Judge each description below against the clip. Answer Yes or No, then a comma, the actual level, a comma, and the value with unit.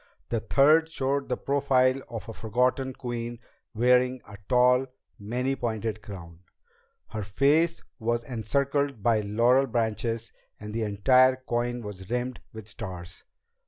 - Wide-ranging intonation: No, average, 3.0 semitones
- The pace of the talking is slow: Yes, slow, 130 wpm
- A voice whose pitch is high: No, low, 120 Hz